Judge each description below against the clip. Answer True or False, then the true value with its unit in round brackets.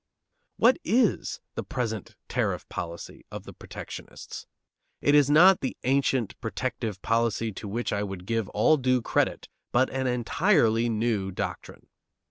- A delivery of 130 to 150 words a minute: True (140 wpm)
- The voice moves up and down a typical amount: True (3.7 semitones)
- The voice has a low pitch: True (120 Hz)